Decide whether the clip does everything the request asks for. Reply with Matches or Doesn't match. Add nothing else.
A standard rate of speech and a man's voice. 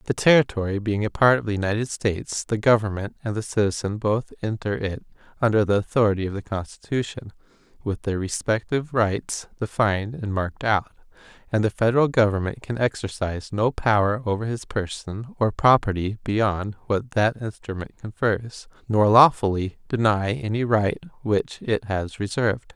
Matches